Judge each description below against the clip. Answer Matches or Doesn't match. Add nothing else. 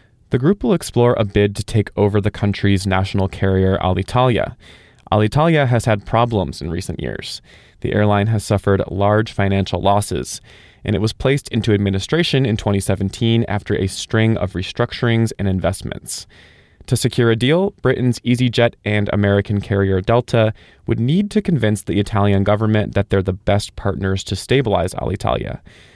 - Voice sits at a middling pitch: Doesn't match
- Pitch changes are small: Doesn't match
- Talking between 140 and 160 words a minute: Matches